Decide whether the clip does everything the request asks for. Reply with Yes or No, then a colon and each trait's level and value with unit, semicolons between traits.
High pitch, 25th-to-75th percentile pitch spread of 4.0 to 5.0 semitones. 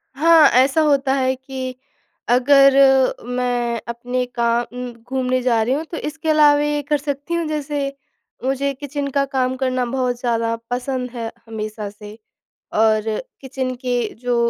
No: very high, 255 Hz; narrow, 2.5 semitones